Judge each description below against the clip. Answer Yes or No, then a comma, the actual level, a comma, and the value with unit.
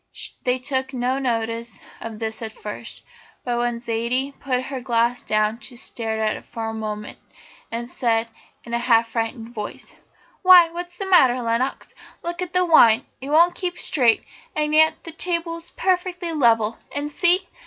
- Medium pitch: No, very high, 250 Hz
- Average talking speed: Yes, average, 170 wpm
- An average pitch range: No, wide, 6.2 semitones